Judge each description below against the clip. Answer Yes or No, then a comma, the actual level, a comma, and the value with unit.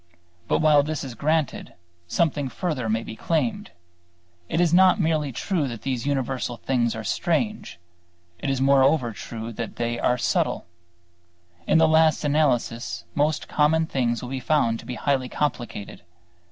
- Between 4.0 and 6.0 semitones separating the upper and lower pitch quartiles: Yes, average, 4.8 semitones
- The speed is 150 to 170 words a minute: Yes, average, 155 wpm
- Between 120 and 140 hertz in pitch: Yes, low, 135 Hz